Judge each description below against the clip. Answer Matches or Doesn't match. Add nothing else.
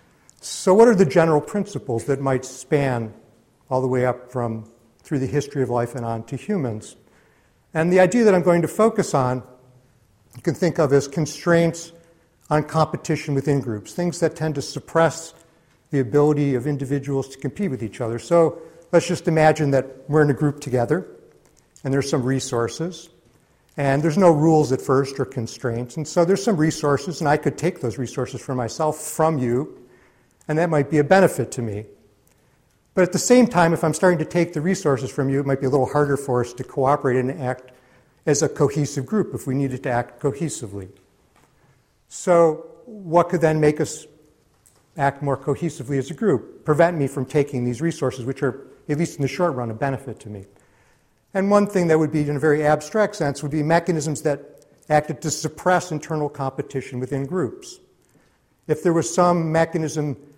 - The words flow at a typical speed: Matches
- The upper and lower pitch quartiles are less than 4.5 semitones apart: Matches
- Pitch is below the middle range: Doesn't match